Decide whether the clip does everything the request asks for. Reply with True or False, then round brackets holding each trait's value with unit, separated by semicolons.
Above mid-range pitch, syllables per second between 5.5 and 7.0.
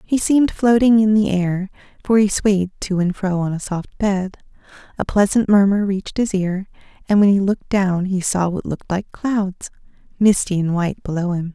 False (195 Hz; 5.0 syllables/s)